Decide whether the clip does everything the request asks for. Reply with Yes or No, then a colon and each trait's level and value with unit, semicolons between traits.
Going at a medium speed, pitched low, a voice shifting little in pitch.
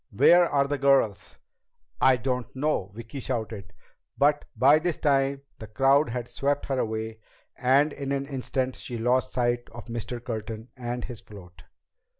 No: average, 155 wpm; low, 125 Hz; average, 3.4 semitones